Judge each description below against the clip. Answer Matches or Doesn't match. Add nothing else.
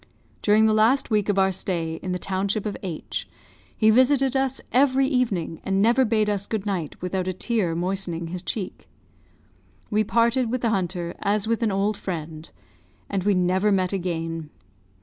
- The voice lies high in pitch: Matches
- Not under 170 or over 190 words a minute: Matches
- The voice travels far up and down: Doesn't match